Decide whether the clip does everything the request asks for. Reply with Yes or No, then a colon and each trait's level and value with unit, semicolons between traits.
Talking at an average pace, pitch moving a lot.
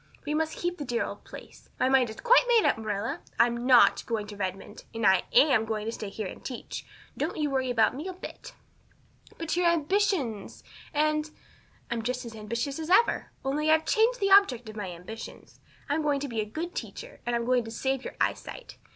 No: fast, 215 wpm; wide, 6.0 semitones